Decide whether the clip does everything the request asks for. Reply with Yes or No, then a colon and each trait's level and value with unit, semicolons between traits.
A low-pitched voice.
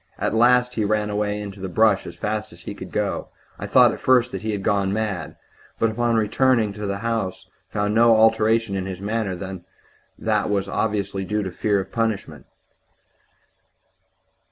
Yes: low, 105 Hz